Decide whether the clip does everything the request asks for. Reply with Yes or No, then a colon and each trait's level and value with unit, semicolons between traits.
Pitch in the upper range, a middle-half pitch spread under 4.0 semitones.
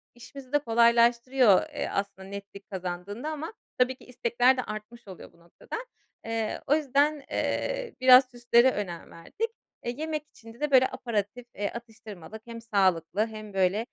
No: high, 235 Hz; average, 4.3 semitones